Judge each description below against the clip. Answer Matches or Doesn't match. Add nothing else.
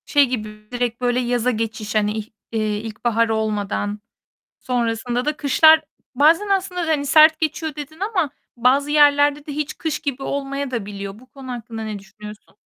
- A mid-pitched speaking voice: Doesn't match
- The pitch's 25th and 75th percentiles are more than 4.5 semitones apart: Matches